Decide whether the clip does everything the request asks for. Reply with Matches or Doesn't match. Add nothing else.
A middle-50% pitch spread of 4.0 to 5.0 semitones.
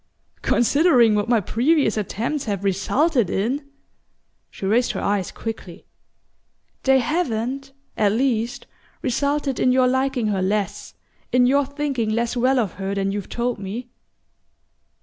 Matches